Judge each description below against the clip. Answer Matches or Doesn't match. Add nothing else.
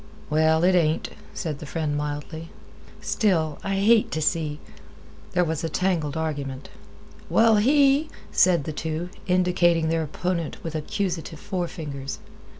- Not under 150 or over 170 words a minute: Doesn't match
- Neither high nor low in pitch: Matches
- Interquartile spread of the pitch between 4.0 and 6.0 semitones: Doesn't match